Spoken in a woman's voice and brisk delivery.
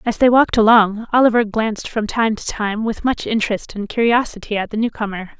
Yes: female; fast, 210 wpm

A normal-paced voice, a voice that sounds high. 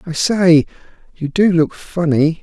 No: average, 150 wpm; medium, 165 Hz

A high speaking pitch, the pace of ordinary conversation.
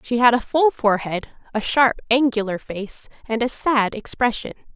Yes: high, 235 Hz; average, 165 wpm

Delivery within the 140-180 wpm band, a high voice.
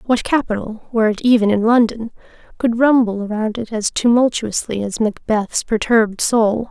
Yes: average, 150 wpm; high, 225 Hz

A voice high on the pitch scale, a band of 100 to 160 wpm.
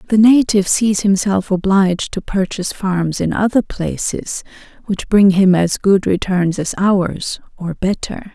Yes: high, 195 Hz; average, 150 wpm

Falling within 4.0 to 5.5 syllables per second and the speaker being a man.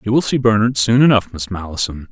No: 6.0 syllables/s; male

